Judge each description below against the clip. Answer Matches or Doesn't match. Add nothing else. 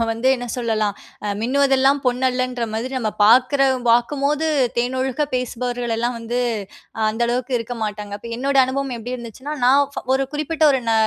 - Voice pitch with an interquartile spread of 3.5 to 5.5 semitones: Doesn't match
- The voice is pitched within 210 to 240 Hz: Doesn't match